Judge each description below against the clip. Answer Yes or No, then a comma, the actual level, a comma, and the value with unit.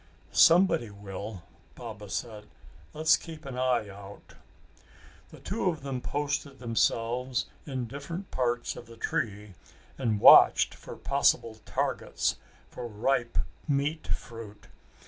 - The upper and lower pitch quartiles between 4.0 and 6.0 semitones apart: Yes, average, 4.6 semitones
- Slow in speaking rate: Yes, slow, 120 wpm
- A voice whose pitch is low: Yes, low, 120 Hz